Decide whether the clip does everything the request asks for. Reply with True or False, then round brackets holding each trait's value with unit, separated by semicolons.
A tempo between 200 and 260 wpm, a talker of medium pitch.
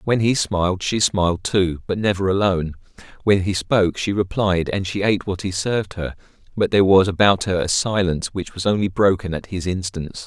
False (205 wpm; 95 Hz)